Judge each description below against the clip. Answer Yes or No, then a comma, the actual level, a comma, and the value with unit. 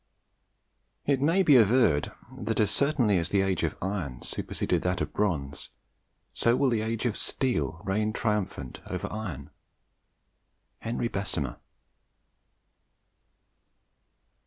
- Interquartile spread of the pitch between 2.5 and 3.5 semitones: No, average, 4.7 semitones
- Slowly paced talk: Yes, slow, 115 wpm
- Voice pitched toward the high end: No, low, 105 Hz